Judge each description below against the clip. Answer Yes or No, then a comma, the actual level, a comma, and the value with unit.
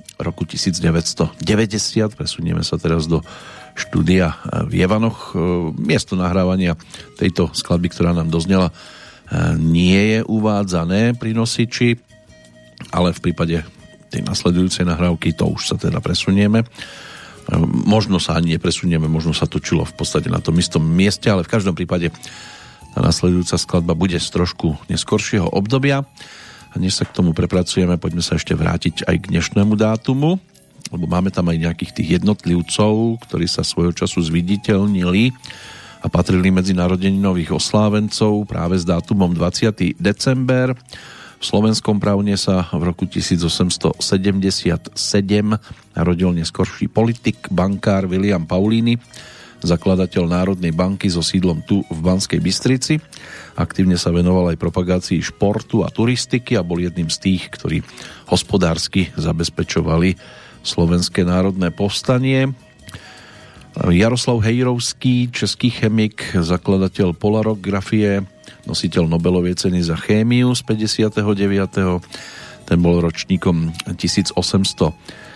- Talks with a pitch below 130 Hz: Yes, very low, 95 Hz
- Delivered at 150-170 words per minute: No, average, 120 wpm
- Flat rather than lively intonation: No, average, 3.5 semitones